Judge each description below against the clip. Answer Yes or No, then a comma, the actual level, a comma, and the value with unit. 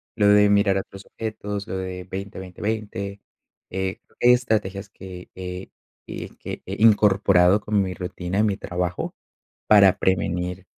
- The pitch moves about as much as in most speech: No, narrow, 2.0 semitones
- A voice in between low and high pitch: No, very low, 95 Hz